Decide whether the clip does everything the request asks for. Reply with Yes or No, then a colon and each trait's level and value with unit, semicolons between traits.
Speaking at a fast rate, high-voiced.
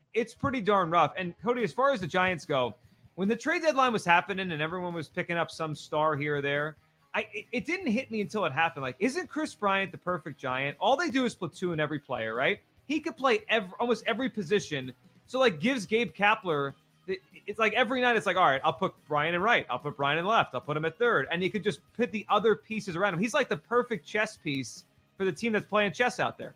Yes: fast, 250 wpm; high, 195 Hz